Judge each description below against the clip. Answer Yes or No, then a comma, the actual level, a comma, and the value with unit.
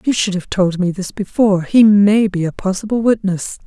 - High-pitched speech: Yes, high, 200 Hz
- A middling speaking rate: No, fast, 215 wpm